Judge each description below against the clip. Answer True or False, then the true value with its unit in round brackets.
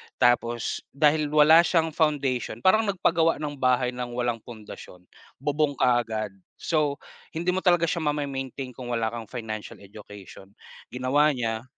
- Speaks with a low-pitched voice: True (130 Hz)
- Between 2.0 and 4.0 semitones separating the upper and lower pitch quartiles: False (4.5 semitones)